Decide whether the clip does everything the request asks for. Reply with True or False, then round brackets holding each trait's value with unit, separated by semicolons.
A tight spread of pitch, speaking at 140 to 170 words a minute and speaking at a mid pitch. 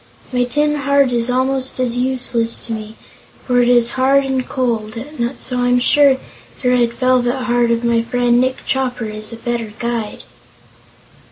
False (1.7 semitones; 165 wpm; 245 Hz)